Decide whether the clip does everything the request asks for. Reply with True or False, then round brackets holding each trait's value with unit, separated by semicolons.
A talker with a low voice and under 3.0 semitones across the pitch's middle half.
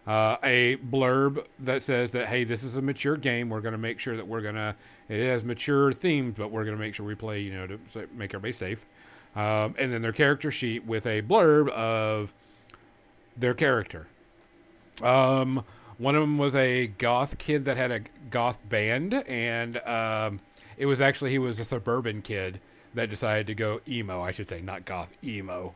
False (120 Hz; 3.4 semitones)